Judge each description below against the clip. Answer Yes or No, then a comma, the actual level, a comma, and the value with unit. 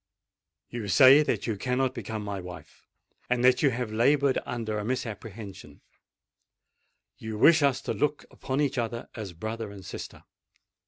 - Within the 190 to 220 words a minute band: No, average, 150 wpm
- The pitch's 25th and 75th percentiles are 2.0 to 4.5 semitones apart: Yes, average, 3.7 semitones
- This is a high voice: No, low, 115 Hz